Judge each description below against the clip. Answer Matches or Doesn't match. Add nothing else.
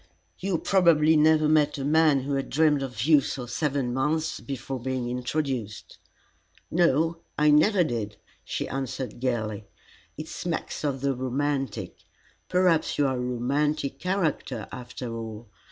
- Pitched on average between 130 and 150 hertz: Matches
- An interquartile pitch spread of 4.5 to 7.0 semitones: Doesn't match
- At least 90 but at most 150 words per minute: Matches